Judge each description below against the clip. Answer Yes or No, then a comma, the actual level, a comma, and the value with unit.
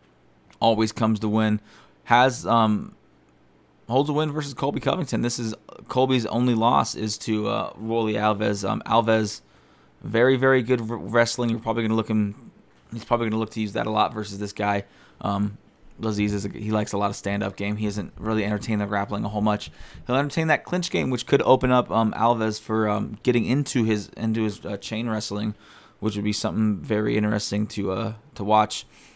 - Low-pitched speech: Yes, low, 110 Hz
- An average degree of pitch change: No, narrow, 2.2 semitones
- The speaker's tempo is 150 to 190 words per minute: No, fast, 205 wpm